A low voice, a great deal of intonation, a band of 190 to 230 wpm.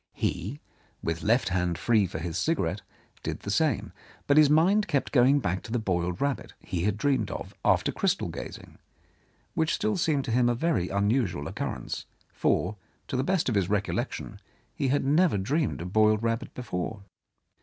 No: low, 115 Hz; wide, 7.0 semitones; average, 175 wpm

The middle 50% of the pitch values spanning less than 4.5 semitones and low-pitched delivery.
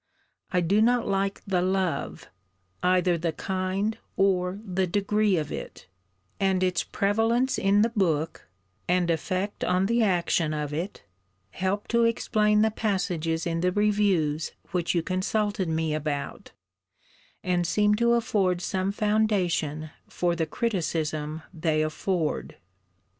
No: average, 3.8 semitones; medium, 185 Hz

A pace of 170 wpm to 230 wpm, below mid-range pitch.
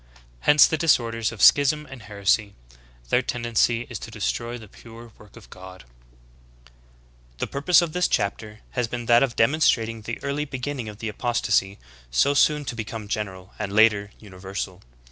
Yes: average, 175 wpm; low, 115 Hz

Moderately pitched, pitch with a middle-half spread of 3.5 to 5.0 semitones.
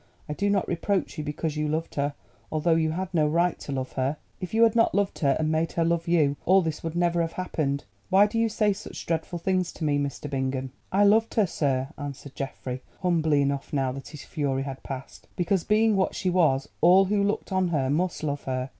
Yes: medium, 160 Hz; average, 4.7 semitones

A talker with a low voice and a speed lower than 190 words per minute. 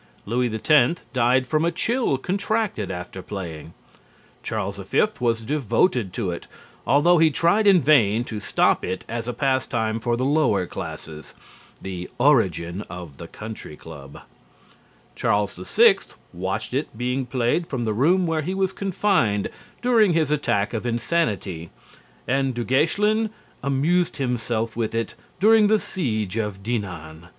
Yes: low, 120 Hz; average, 145 wpm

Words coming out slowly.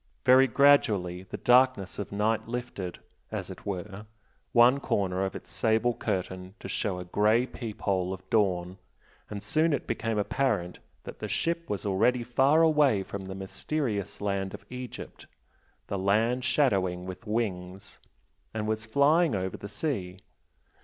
No: average, 155 wpm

